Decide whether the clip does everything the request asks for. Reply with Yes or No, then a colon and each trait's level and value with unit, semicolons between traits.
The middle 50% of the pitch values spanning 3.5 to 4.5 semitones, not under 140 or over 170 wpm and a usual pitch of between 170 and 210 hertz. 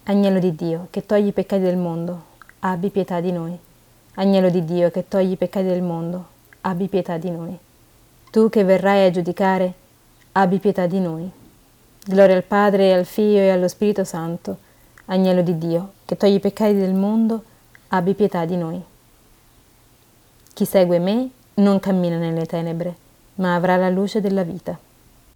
No: narrow, 2.4 semitones; average, 165 wpm; medium, 185 Hz